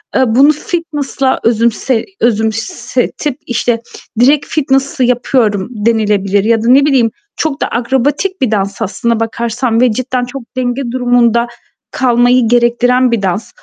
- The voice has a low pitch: No, high, 245 Hz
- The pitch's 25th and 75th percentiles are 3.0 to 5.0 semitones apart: No, narrow, 2.6 semitones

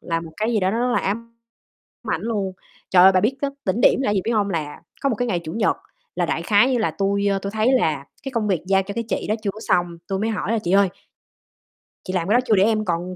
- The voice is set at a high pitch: Yes, high, 200 Hz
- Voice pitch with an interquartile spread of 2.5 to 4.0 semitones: Yes, average, 3.5 semitones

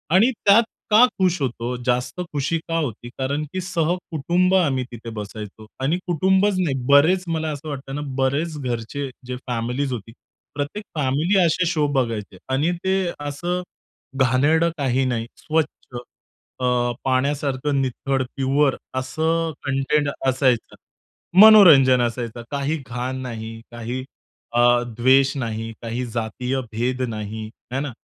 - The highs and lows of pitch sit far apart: No, average, 4.7 semitones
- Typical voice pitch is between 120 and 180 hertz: Yes, low, 135 Hz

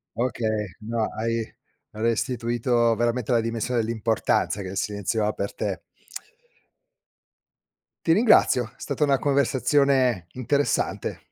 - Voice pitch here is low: Yes, low, 115 Hz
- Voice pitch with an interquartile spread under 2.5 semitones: No, average, 2.8 semitones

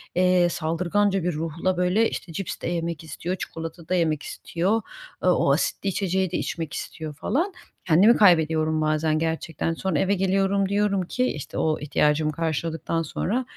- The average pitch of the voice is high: No, medium, 170 Hz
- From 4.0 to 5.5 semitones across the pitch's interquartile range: No, average, 3.2 semitones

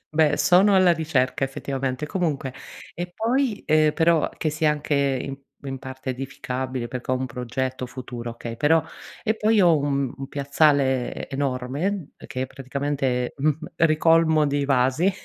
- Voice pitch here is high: No, medium, 140 Hz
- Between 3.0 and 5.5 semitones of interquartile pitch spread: Yes, average, 3.5 semitones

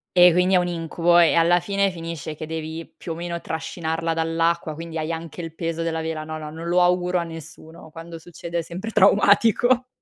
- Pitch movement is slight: Yes, narrow, 1.5 semitones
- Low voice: No, medium, 165 Hz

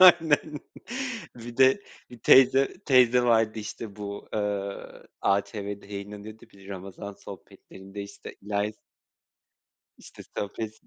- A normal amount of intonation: Yes, average, 3.3 semitones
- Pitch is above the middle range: No, low, 105 Hz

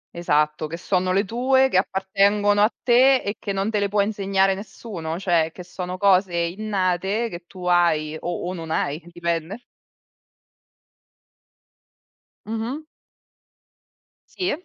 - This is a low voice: No, high, 190 Hz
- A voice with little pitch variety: No, average, 3.3 semitones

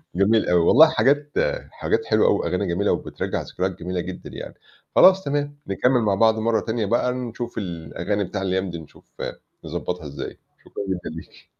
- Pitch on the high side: No, low, 100 Hz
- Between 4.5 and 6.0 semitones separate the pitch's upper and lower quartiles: Yes, wide, 5.4 semitones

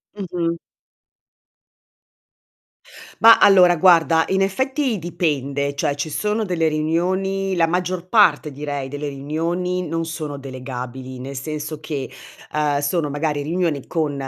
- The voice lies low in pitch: No, medium, 160 Hz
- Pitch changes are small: No, average, 4.1 semitones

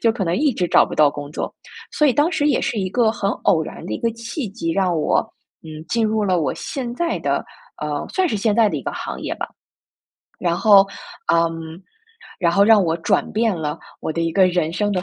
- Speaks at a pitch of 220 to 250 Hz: No, high, 195 Hz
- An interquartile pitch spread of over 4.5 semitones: Yes, wide, 5.6 semitones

